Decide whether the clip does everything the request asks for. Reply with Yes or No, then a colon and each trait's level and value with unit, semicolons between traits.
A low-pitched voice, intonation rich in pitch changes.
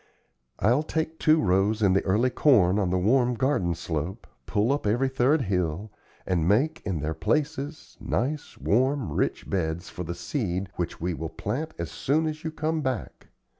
Yes: low, 110 Hz; wide, 8.0 semitones